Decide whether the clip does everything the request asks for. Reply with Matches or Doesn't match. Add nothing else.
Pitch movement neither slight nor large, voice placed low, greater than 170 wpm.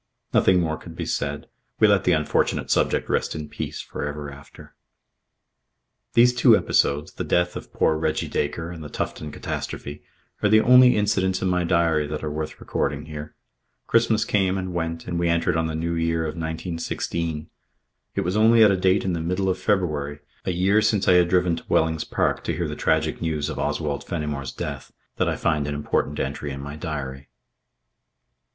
Matches